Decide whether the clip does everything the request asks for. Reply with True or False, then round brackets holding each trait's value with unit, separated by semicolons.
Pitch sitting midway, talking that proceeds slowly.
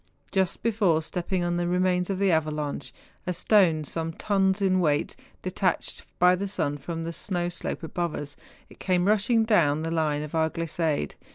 False (175 Hz; 170 wpm)